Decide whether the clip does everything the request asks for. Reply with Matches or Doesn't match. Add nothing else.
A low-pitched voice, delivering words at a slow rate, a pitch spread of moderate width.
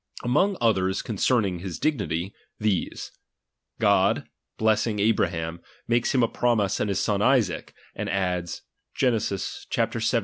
Matches